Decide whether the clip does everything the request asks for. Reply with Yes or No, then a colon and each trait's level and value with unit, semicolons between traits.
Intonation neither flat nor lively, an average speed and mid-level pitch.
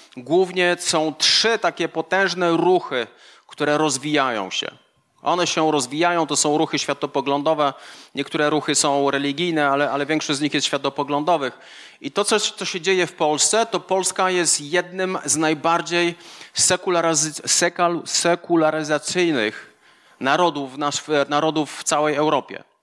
Yes: average, 3.1 semitones; average, 125 wpm; medium, 155 Hz